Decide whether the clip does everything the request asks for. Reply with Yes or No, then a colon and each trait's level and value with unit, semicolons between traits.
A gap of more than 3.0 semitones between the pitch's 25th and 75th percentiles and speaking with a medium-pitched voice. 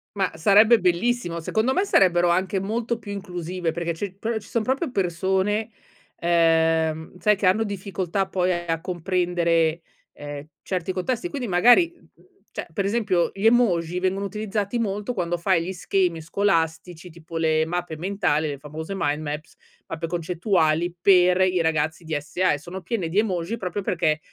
Yes: average, 3.5 semitones; medium, 180 Hz